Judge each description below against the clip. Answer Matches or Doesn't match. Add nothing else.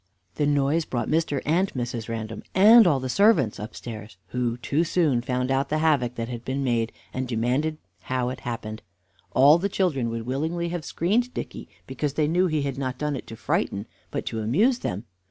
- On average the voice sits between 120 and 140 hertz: Matches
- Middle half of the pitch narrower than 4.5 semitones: Doesn't match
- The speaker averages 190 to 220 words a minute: Matches